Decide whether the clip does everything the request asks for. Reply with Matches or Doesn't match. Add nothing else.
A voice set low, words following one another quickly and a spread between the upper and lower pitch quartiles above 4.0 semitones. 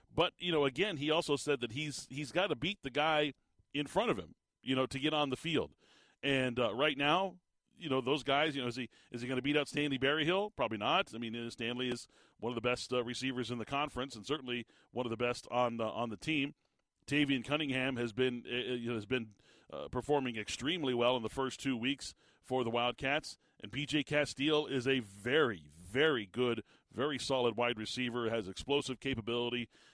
Doesn't match